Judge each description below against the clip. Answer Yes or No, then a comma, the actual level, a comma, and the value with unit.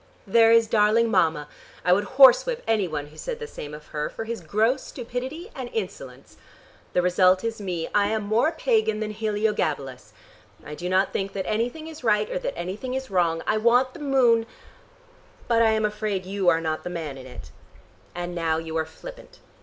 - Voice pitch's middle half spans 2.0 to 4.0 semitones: No, average, 5.0 semitones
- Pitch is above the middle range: Yes, high, 210 Hz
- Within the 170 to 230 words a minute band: Yes, average, 200 wpm